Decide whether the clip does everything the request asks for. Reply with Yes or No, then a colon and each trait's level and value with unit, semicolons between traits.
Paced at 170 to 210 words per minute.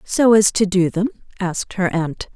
Yes: fast, 205 wpm